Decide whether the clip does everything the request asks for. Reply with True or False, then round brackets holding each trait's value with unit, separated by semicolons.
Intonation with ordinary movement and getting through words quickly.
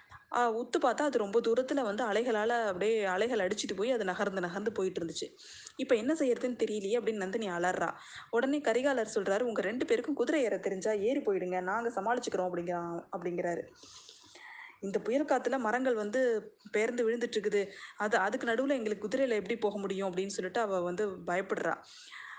True (4.1 semitones; 160 wpm)